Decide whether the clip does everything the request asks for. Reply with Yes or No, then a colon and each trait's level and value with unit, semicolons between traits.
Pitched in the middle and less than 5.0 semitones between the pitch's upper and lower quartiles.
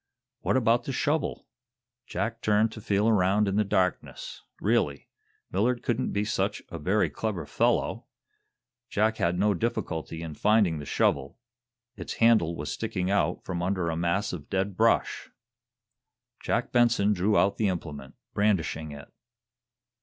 No: low, 100 Hz; average, 4.2 semitones